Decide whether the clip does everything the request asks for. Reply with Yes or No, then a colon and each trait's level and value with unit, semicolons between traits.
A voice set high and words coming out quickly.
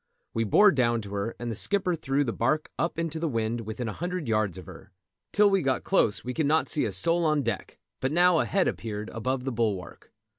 No: low, 130 Hz; fast, 235 wpm